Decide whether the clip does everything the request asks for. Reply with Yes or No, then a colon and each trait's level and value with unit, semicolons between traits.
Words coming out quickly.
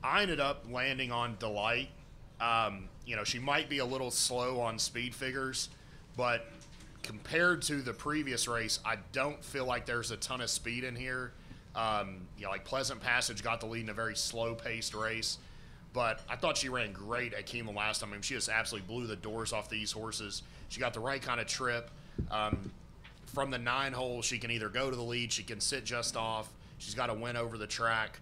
Yes: fast, 215 wpm